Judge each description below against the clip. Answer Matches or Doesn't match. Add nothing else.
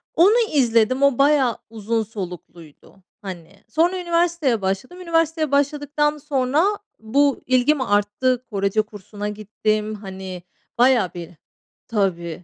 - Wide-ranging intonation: Matches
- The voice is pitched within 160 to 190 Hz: Doesn't match